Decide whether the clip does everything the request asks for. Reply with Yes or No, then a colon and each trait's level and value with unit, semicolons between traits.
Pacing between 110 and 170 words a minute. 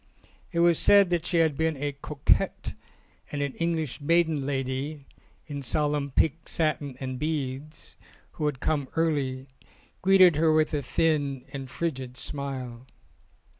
Yes: average, 140 wpm